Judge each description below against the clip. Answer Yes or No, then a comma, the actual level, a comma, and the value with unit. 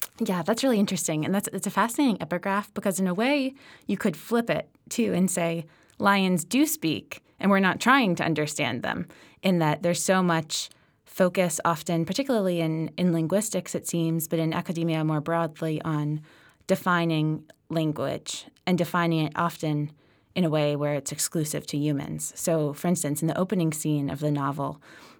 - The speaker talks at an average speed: Yes, average, 175 wpm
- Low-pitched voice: No, medium, 170 Hz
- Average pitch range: Yes, average, 3.6 semitones